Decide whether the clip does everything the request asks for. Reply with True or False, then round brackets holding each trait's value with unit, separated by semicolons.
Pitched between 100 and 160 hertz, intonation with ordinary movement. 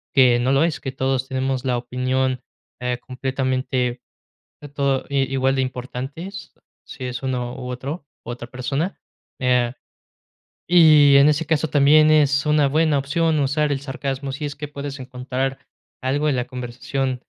False (135 Hz; 2.2 semitones)